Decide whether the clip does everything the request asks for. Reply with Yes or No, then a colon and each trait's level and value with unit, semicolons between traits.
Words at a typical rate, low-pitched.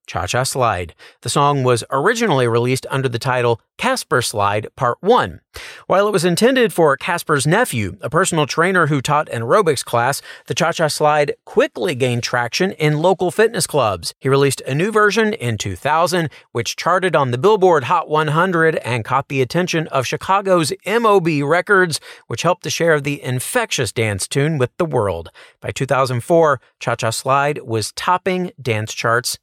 No: average, 170 wpm; medium, 145 Hz